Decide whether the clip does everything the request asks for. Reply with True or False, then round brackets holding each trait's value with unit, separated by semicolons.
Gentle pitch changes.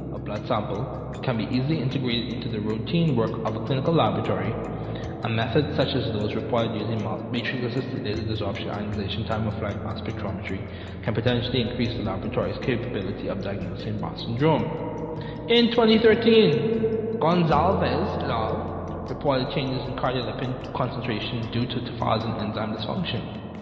False (3.8 semitones)